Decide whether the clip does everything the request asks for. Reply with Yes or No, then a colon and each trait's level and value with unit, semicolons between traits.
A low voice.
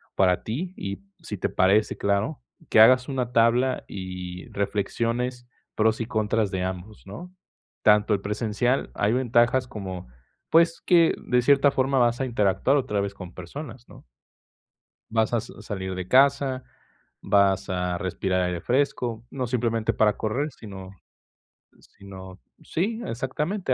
Yes: low, 110 Hz